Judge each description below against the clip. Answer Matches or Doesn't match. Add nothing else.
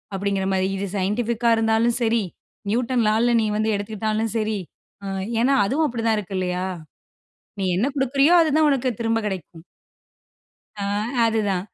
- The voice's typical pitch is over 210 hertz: Matches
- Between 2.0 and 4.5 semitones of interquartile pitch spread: Matches